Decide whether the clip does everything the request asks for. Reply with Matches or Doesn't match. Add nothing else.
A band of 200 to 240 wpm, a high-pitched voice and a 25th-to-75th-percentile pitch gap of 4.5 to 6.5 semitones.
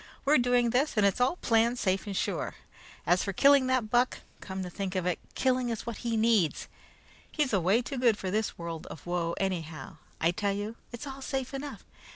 Matches